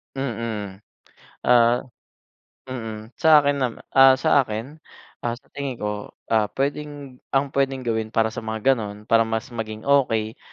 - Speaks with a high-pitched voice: No, low, 120 Hz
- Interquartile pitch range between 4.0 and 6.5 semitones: No, average, 3.4 semitones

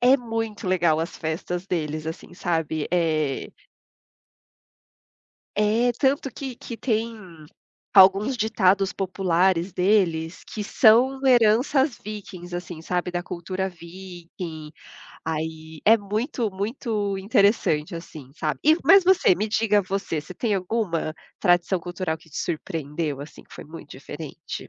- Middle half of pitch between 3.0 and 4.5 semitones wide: No, average, 5.0 semitones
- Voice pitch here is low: No, medium, 185 Hz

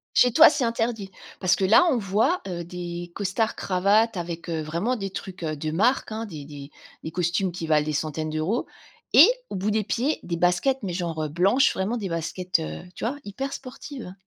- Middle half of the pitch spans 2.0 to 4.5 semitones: No, average, 5.2 semitones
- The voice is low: No, medium, 185 Hz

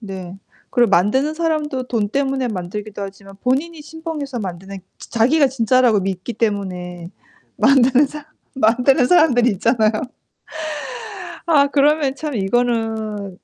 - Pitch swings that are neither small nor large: No, wide, 5.7 semitones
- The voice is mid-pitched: No, high, 240 Hz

